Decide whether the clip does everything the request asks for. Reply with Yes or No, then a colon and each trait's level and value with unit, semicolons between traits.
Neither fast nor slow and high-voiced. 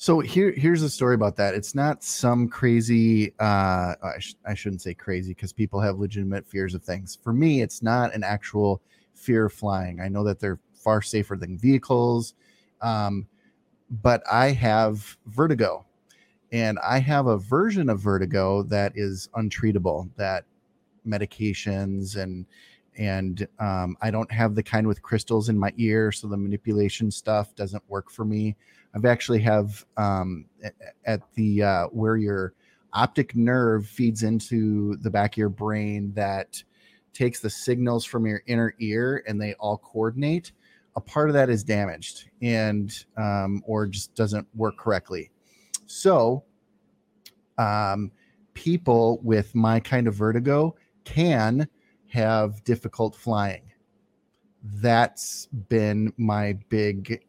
No: average, 145 wpm; low, 110 Hz